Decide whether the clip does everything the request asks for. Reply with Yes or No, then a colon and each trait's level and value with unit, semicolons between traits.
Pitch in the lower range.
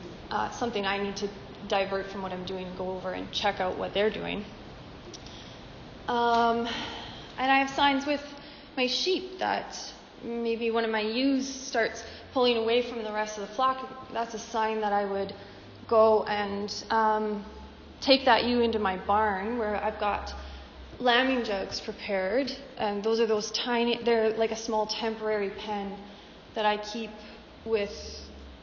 No: high, 220 Hz